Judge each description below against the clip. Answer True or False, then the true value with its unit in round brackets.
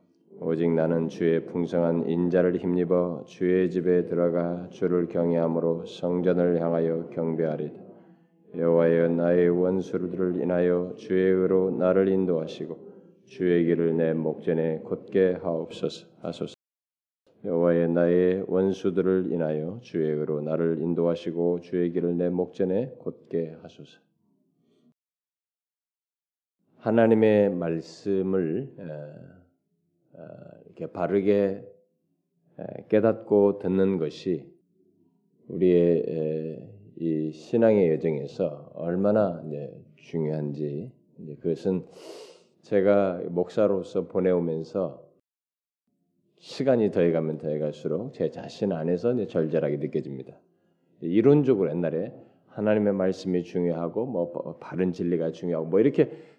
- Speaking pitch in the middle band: False (85 Hz)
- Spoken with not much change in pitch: True (2.3 semitones)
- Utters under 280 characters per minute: True (245 characters per minute)